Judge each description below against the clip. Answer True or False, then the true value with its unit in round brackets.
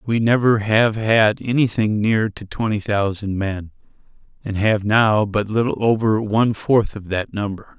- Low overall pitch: True (105 Hz)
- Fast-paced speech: False (160 wpm)